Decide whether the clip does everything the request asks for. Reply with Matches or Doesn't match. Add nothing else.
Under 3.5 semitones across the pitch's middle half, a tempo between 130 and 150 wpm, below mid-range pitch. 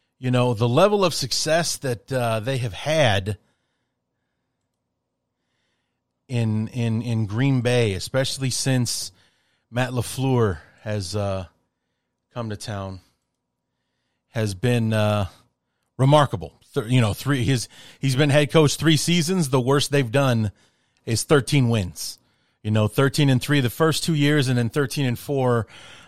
Doesn't match